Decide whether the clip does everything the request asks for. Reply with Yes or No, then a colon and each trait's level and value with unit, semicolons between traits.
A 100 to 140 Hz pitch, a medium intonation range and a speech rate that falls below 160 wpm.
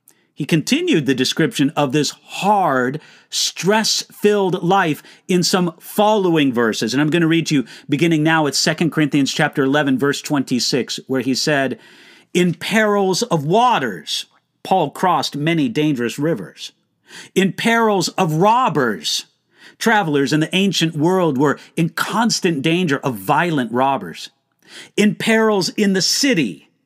No: medium, 165 Hz; average, 5.0 semitones; average, 140 wpm